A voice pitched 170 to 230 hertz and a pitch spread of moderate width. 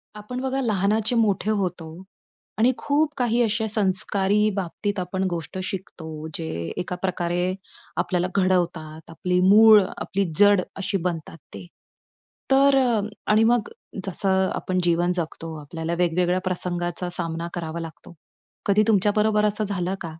Yes: high, 190 Hz; average, 3.4 semitones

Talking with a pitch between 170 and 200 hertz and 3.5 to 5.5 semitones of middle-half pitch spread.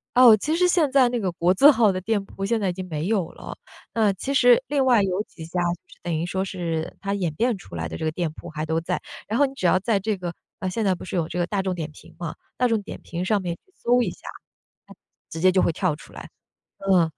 Yes: high, 190 Hz; average, 4.7 semitones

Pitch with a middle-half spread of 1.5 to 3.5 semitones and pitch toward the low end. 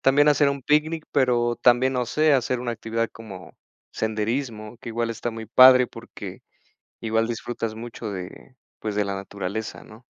Yes: average, 2.7 semitones; low, 115 Hz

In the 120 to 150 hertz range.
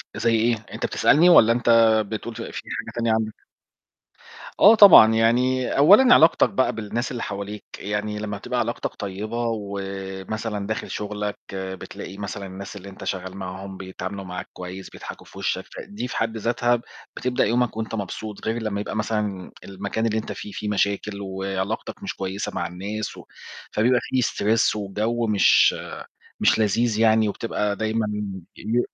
No: low, 105 Hz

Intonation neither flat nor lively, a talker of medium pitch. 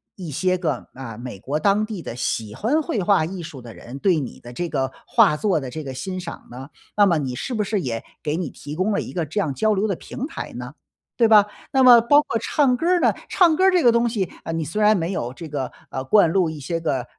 No: wide, 7.8 semitones; medium, 175 Hz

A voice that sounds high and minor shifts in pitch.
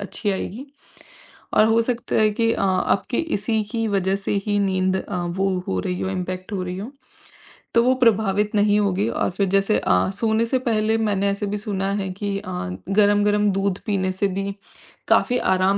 Yes: high, 200 Hz; narrow, 2.0 semitones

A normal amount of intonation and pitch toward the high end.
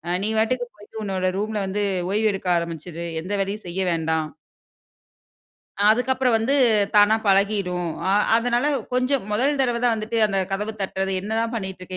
Yes: average, 3.3 semitones; high, 210 Hz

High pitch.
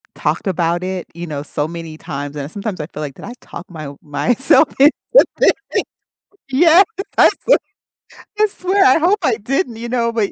Yes: high, 195 Hz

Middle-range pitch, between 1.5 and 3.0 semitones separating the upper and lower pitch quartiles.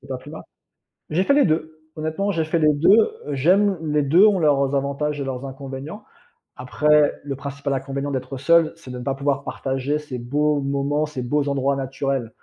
Yes: medium, 145 Hz; narrow, 2.4 semitones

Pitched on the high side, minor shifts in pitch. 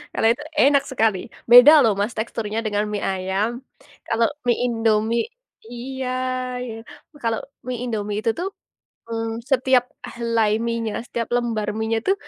Yes: high, 230 Hz; narrow, 2.0 semitones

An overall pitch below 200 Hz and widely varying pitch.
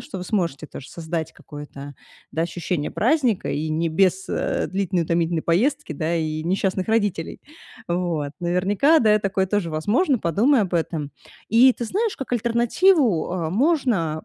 Yes: medium, 185 Hz; wide, 5.9 semitones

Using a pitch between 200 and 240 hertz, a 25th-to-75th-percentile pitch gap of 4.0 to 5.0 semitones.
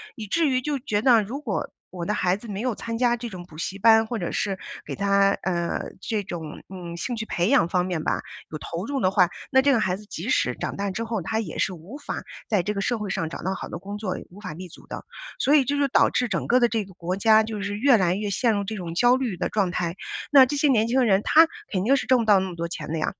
Yes: high, 205 Hz; average, 4.5 semitones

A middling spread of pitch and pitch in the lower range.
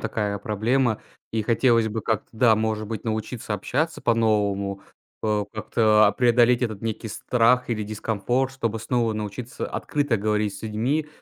No: narrow, 2.2 semitones; low, 110 Hz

